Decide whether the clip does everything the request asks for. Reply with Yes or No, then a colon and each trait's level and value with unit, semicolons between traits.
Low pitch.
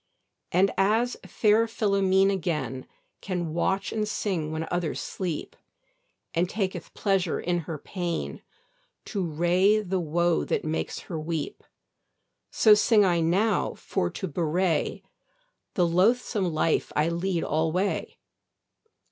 No: medium, 180 Hz